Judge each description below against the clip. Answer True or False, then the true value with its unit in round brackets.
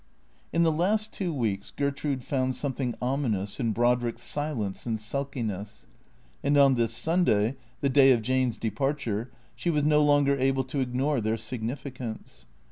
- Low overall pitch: True (130 Hz)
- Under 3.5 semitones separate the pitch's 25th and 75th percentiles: False (3.8 semitones)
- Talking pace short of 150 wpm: False (155 wpm)